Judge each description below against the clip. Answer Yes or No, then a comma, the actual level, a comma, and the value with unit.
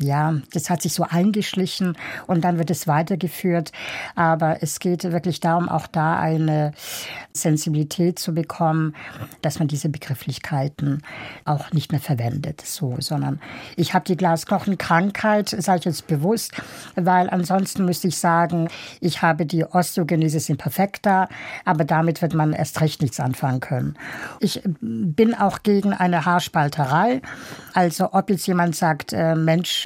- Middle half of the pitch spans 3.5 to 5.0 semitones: No, average, 3.0 semitones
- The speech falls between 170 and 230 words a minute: No, average, 145 wpm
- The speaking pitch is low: No, medium, 165 Hz